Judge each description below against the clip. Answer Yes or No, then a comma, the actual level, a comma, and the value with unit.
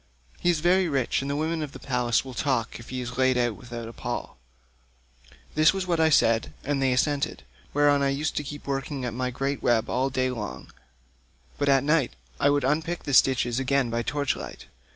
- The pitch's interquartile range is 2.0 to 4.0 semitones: Yes, average, 2.8 semitones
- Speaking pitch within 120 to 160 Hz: Yes, low, 135 Hz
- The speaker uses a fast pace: Yes, fast, 215 wpm